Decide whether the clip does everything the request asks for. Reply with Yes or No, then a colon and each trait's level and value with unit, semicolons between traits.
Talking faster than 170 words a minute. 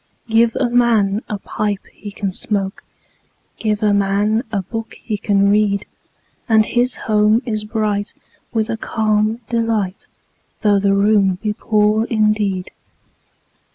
No: average, 140 wpm